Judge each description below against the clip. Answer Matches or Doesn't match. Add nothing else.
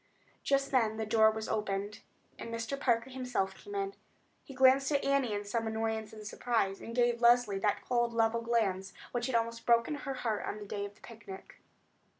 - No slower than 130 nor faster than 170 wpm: Doesn't match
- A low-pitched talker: Doesn't match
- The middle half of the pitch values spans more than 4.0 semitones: Doesn't match